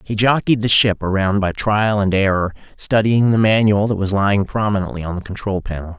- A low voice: Yes, low, 100 Hz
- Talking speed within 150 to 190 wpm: No, average, 200 wpm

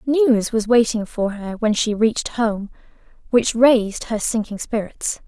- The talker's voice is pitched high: Yes, high, 225 Hz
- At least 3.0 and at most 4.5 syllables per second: Yes, 4.3 syllables/s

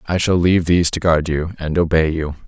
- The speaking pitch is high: No, very low, 85 Hz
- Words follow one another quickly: Yes, fast, 245 wpm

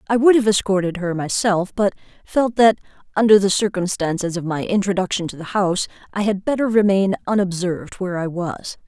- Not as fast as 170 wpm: No, average, 175 wpm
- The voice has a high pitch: Yes, high, 195 Hz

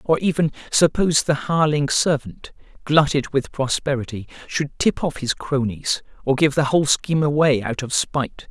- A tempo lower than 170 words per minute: Yes, average, 160 wpm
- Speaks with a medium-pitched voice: Yes, medium, 145 Hz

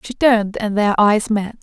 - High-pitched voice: Yes, high, 215 Hz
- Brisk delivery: Yes, fast, 220 wpm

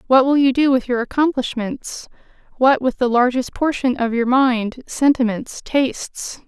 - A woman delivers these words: Yes, female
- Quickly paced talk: No, average, 140 wpm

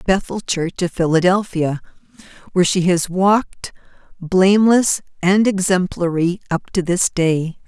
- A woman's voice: Yes, female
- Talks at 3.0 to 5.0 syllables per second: Yes, 4.3 syllables/s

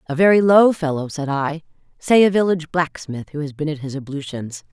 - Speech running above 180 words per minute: Yes, fast, 205 wpm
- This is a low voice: No, medium, 155 Hz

